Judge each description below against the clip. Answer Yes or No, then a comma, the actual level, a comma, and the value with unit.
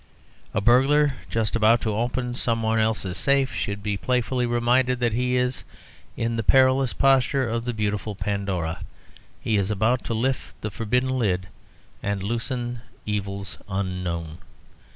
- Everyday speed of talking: Yes, average, 150 wpm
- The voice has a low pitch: Yes, low, 115 Hz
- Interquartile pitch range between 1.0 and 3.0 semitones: No, average, 3.7 semitones